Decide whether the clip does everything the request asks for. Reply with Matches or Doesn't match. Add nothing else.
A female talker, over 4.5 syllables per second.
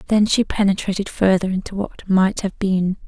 Matches